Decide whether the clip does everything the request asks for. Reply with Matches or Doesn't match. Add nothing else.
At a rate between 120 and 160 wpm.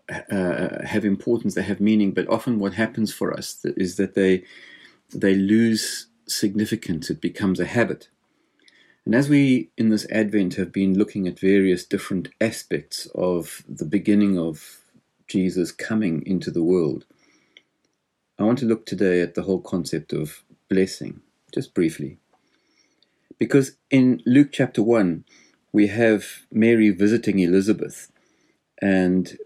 Matches